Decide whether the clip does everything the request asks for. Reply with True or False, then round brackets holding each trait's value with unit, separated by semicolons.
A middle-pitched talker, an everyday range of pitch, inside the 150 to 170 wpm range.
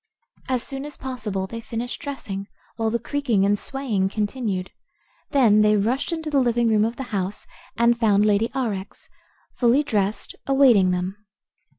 False (225 Hz; 4.3 semitones; 160 wpm)